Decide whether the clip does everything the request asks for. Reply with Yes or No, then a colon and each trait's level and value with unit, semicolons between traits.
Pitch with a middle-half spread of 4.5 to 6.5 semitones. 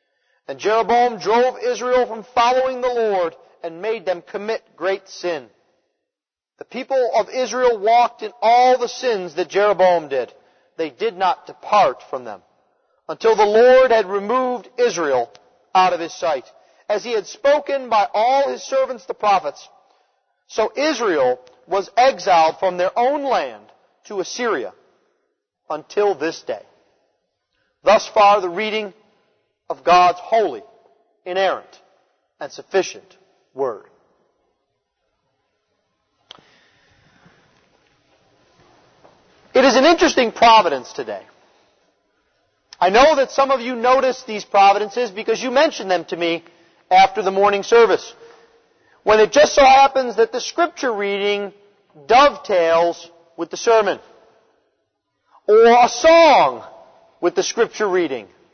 Yes: average, 5.3 semitones